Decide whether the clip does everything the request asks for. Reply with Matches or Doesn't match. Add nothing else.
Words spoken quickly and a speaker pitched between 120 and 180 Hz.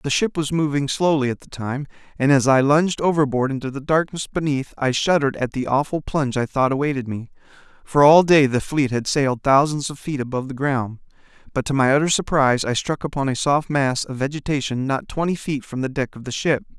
Matches